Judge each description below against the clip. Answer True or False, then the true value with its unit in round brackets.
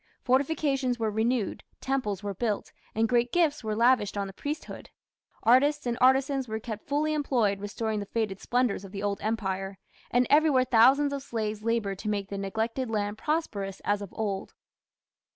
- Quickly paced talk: False (170 wpm)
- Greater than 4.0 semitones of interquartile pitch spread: True (4.4 semitones)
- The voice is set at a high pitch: True (225 Hz)